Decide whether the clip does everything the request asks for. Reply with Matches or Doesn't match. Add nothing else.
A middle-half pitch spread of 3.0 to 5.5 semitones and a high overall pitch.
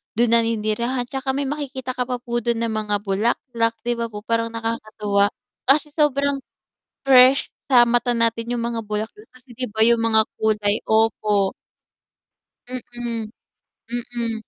Doesn't match